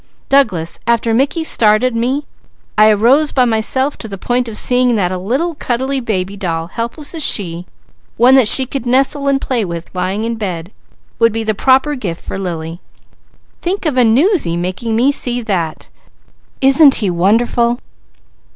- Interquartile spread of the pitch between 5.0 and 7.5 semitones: Yes, average, 5.3 semitones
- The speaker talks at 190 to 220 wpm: No, average, 170 wpm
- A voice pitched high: Yes, high, 230 Hz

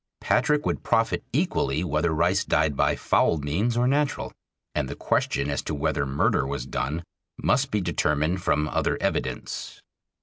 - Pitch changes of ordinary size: No, wide, 8.8 semitones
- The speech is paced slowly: No, average, 160 wpm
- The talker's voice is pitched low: Yes, very low, 80 Hz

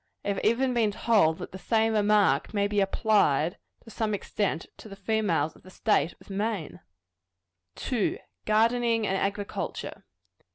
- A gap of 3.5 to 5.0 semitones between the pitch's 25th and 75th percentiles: No, narrow, 2.5 semitones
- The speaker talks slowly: No, average, 155 wpm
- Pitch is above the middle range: Yes, high, 210 Hz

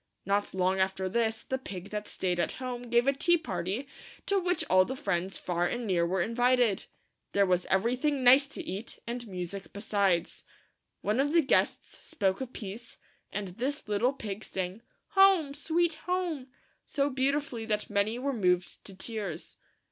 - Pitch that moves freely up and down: Yes, wide, 5.8 semitones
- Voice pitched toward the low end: No, high, 225 Hz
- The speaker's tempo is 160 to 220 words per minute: Yes, average, 175 wpm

